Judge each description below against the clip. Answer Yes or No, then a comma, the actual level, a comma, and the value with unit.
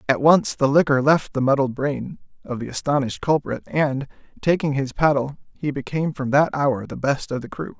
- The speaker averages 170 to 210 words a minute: Yes, average, 200 wpm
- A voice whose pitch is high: No, medium, 140 Hz